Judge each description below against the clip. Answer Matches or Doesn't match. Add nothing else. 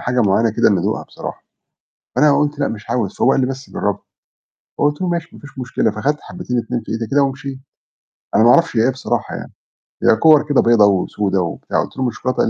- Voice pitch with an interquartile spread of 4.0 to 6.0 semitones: Matches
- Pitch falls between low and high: Doesn't match